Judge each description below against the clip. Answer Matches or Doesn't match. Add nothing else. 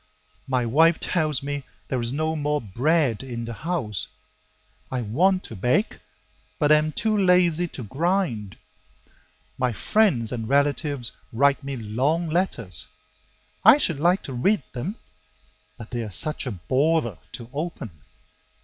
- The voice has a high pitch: Doesn't match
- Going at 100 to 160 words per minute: Matches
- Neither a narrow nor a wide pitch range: Doesn't match